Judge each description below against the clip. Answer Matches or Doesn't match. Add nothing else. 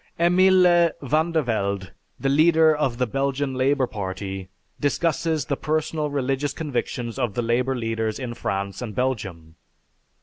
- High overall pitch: Doesn't match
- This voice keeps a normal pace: Doesn't match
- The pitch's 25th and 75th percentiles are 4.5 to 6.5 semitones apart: Matches